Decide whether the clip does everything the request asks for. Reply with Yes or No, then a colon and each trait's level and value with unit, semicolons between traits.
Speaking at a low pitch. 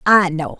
No: medium, 170 Hz